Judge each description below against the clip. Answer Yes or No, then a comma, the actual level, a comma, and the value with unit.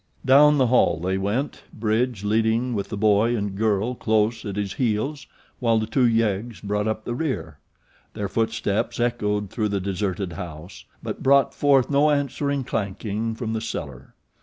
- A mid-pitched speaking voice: No, low, 110 Hz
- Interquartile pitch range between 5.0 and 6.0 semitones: No, average, 3.3 semitones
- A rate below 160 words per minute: No, average, 165 wpm